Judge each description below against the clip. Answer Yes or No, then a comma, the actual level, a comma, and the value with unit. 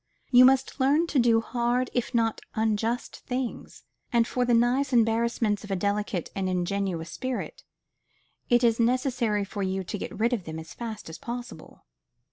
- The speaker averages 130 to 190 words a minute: Yes, average, 170 wpm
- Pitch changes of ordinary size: Yes, average, 3.4 semitones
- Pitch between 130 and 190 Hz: No, high, 230 Hz